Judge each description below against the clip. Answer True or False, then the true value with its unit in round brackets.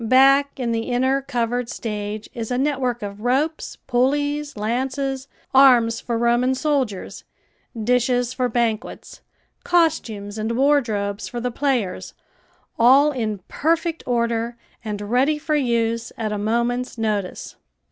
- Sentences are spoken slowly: True (125 wpm)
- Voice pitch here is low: False (245 Hz)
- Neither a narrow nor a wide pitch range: True (3.1 semitones)